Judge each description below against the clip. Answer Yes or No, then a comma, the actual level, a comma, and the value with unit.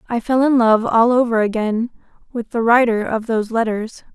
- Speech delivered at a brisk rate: No, average, 175 wpm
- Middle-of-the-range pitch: No, high, 230 Hz